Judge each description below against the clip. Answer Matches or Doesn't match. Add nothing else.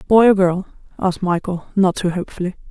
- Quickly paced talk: Doesn't match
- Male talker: Doesn't match